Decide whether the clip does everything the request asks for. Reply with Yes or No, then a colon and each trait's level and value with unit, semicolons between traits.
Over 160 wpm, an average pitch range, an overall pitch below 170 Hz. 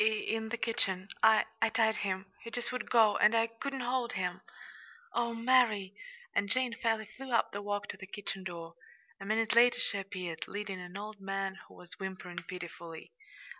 No: average, 185 wpm; average, 3.4 semitones; high, 210 Hz